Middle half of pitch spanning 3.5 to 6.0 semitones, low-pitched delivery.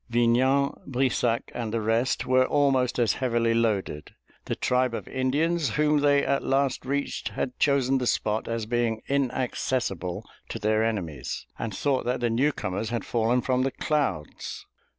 No: average, 3.0 semitones; low, 125 Hz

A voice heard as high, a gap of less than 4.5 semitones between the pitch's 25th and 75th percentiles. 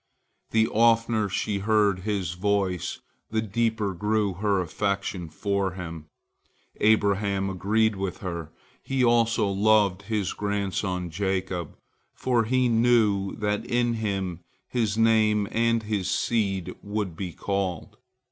No: low, 100 Hz; narrow, 2.6 semitones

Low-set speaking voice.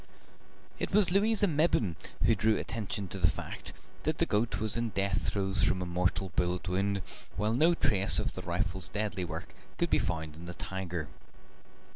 Yes: very low, 95 Hz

